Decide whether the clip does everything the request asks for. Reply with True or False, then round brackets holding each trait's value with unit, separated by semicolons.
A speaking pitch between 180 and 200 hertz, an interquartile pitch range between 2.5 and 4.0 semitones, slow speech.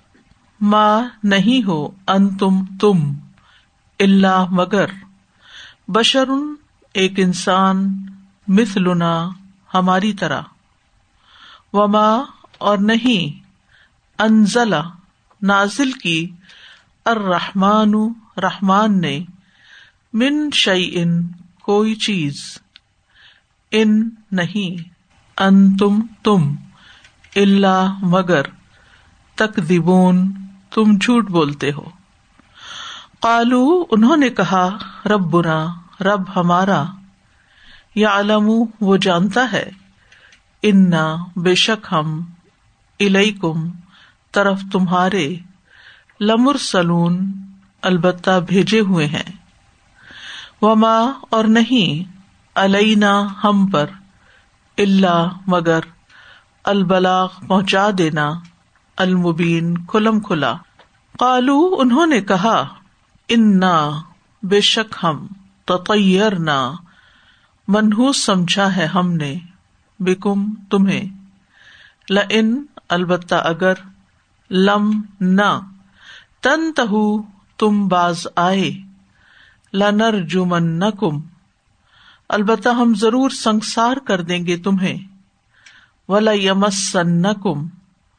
True (195 Hz; 2.9 semitones; 75 wpm)